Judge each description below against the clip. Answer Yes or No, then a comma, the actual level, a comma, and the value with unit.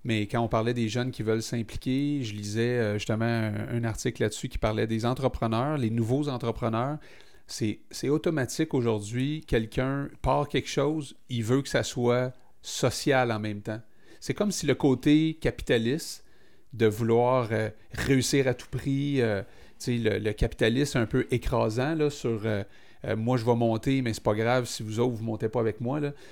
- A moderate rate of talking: Yes, average, 185 wpm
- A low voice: Yes, low, 120 Hz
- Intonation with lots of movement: No, average, 3.2 semitones